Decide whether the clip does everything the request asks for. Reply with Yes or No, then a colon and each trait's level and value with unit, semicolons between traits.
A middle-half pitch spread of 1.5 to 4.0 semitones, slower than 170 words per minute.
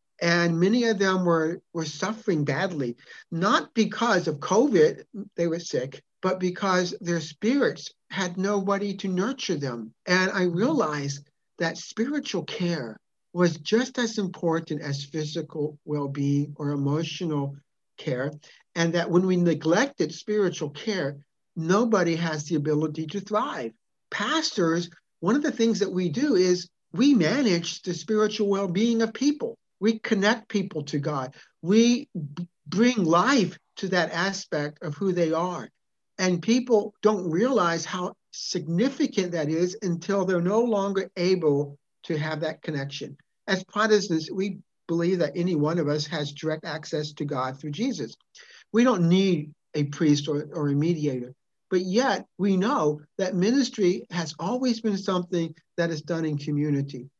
No: average, 4.6 semitones; average, 150 wpm